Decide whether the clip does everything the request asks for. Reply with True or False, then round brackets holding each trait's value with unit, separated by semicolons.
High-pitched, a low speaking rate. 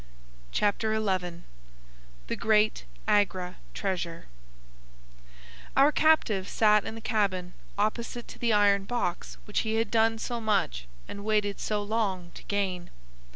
True (205 Hz; 130 wpm)